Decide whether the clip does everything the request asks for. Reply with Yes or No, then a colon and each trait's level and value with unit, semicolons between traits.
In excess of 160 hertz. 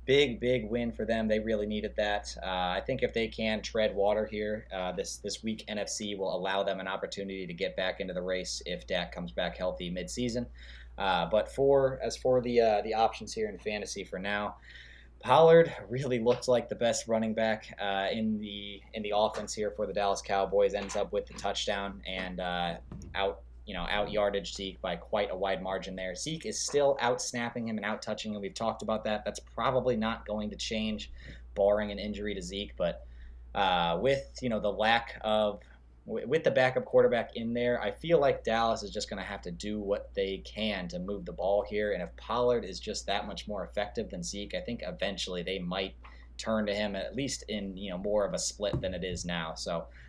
No: low, 105 Hz